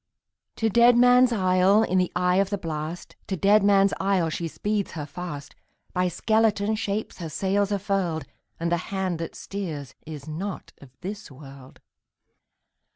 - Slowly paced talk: No, average, 155 wpm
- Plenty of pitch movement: No, average, 3.7 semitones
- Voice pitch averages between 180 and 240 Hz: Yes, high, 190 Hz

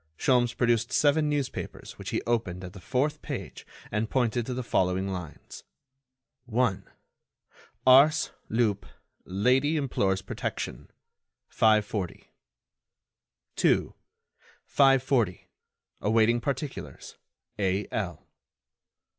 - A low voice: Yes, low, 115 Hz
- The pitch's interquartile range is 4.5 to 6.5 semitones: Yes, average, 5.1 semitones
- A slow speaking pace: Yes, slow, 90 wpm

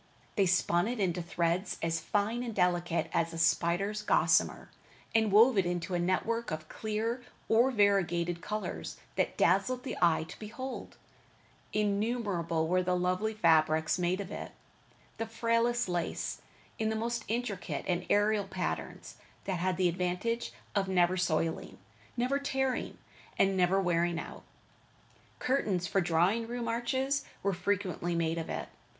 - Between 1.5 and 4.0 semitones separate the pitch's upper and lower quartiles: No, average, 4.5 semitones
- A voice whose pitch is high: Yes, high, 195 Hz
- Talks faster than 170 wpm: No, average, 145 wpm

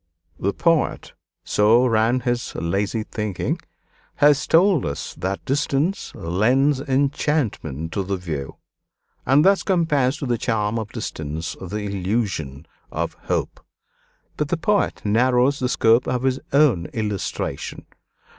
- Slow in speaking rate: Yes, slow, 125 wpm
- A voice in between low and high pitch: No, low, 120 Hz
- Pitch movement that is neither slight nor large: No, wide, 6.1 semitones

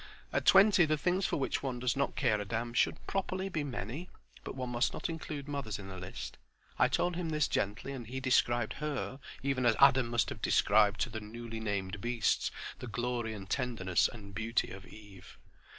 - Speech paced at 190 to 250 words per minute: Yes, average, 200 wpm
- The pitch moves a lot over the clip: No, average, 4.5 semitones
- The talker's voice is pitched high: No, low, 120 Hz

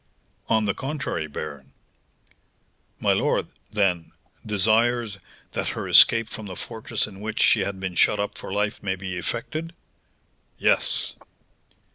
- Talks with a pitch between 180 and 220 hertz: No, low, 105 Hz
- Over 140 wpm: No, slow, 135 wpm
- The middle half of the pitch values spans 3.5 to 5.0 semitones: No, average, 2.9 semitones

